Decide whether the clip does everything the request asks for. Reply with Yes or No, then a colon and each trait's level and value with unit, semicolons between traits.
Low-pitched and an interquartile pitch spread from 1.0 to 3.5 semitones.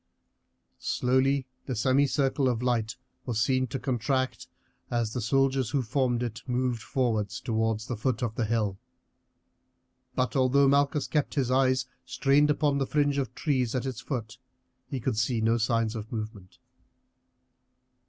Yes: low, 125 Hz; average, 3.1 semitones